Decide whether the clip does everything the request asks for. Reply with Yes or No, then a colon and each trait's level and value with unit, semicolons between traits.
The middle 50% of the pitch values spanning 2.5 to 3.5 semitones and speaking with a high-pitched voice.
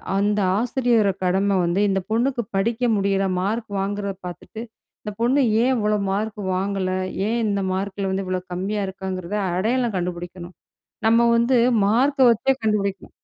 Yes: average, 3.2 semitones; high, 200 Hz